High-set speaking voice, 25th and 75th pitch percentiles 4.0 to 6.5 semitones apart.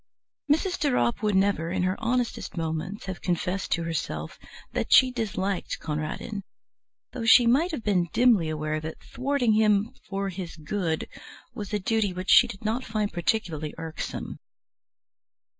Yes: high, 195 Hz; average, 5.1 semitones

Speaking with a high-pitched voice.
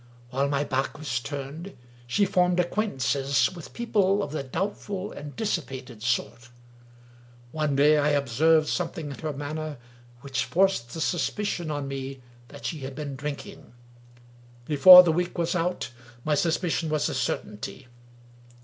No: medium, 150 Hz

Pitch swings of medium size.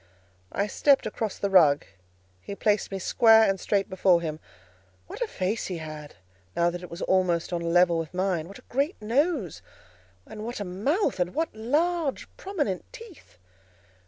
No: wide, 6.0 semitones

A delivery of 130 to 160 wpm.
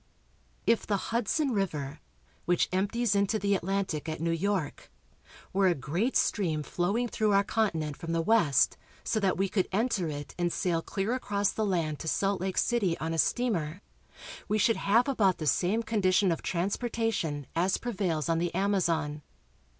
No: average, 175 wpm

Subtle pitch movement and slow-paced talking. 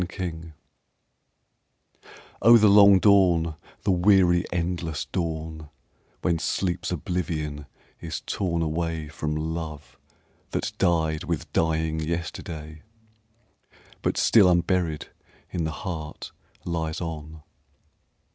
Yes: narrow, 2.1 semitones; slow, 100 wpm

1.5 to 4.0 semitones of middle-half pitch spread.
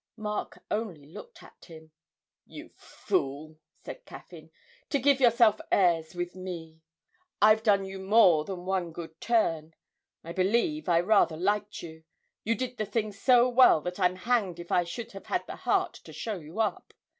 No: average, 4.8 semitones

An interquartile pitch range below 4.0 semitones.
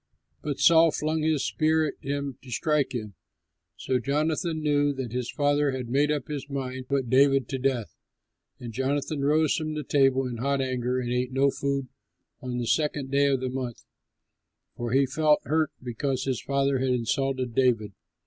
Yes: narrow, 2.4 semitones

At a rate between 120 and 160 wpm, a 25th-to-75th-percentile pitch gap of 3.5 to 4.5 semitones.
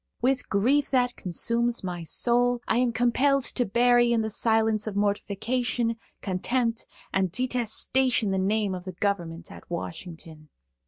Yes: average, 145 wpm; average, 4.1 semitones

